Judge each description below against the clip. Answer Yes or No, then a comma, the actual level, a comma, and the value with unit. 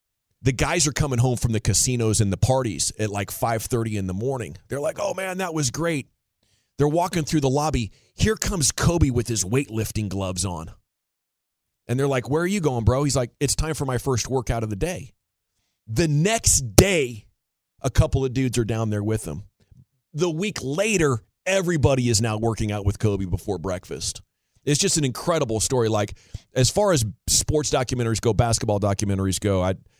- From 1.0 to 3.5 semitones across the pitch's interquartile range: No, average, 5.3 semitones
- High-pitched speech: No, low, 120 Hz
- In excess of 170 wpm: Yes, average, 190 wpm